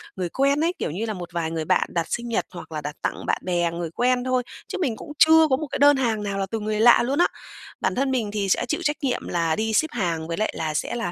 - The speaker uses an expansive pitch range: Yes, wide, 7.2 semitones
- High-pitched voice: Yes, high, 215 Hz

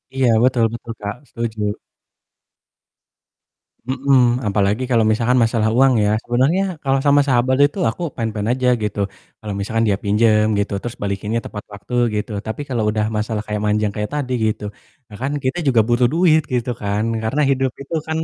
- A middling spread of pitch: Yes, average, 3.5 semitones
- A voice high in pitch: No, low, 115 Hz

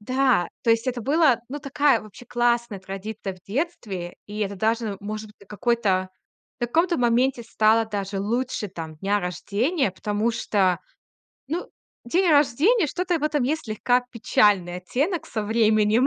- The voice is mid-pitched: No, high, 225 Hz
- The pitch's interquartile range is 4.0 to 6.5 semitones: Yes, average, 4.4 semitones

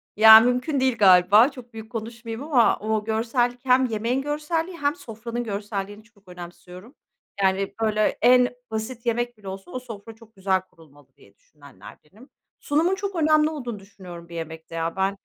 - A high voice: Yes, high, 225 Hz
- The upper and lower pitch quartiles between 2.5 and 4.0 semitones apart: No, average, 4.4 semitones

